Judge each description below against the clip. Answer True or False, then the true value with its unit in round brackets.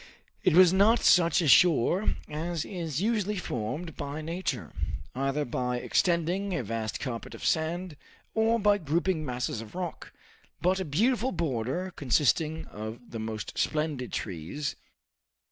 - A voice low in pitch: False (160 Hz)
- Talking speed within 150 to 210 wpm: False (140 wpm)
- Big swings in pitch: True (6.4 semitones)